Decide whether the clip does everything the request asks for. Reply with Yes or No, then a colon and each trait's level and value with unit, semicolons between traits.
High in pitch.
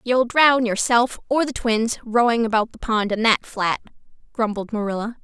Yes: high, 230 Hz